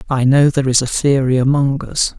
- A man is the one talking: Yes, male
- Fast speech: Yes, fast, 220 wpm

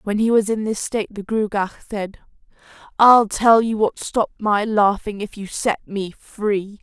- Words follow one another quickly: No, average, 185 wpm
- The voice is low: No, high, 210 Hz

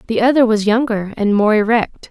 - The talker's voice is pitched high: Yes, high, 220 Hz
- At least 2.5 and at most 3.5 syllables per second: No, 5.3 syllables/s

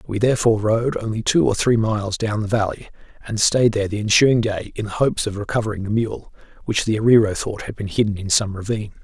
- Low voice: Yes, low, 110 Hz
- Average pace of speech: No, fast, 220 wpm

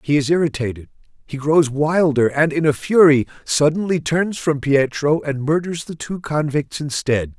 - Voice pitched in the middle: Yes, medium, 150 Hz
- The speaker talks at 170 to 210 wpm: No, average, 160 wpm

